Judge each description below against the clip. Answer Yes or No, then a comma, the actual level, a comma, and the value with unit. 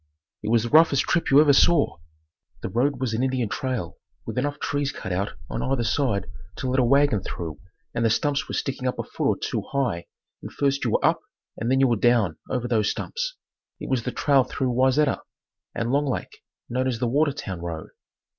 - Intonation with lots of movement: No, average, 3.4 semitones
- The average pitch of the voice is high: No, low, 130 Hz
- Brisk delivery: Yes, fast, 210 wpm